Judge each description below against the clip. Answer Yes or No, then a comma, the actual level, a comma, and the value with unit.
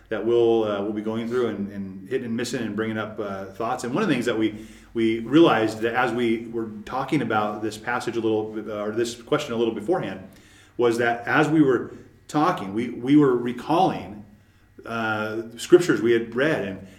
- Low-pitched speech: Yes, low, 115 Hz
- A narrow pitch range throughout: Yes, narrow, 1.8 semitones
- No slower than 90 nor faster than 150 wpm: No, fast, 205 wpm